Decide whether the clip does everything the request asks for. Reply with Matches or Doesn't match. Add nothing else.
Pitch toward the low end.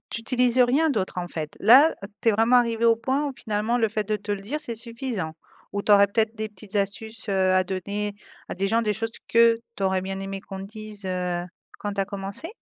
Doesn't match